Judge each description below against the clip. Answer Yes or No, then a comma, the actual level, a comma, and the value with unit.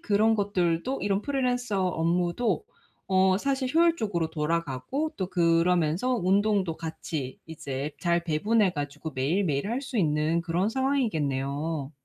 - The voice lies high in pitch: No, medium, 180 Hz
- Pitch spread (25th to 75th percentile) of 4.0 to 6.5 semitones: Yes, average, 5.3 semitones